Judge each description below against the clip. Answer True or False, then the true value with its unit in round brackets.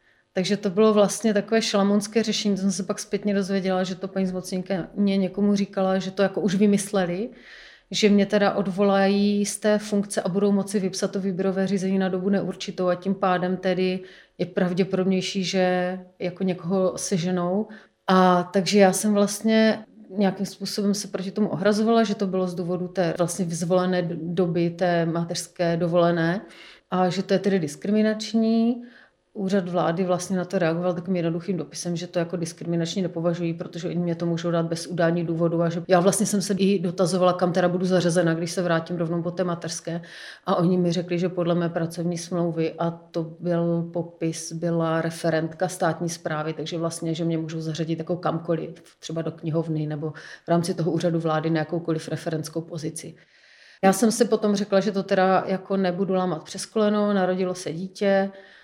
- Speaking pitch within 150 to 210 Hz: True (185 Hz)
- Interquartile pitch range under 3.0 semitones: True (2.5 semitones)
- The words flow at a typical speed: False (180 wpm)